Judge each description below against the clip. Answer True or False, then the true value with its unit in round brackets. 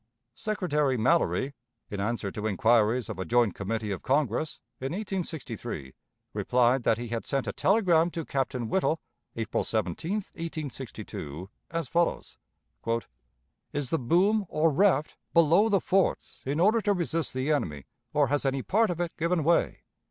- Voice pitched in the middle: True (145 Hz)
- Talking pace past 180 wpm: False (150 wpm)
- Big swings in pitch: True (6.5 semitones)